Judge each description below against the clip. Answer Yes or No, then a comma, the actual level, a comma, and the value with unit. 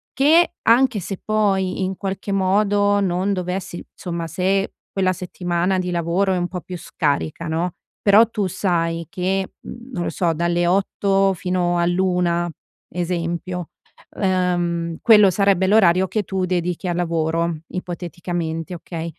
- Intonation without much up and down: Yes, narrow, 2.2 semitones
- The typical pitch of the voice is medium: Yes, medium, 180 Hz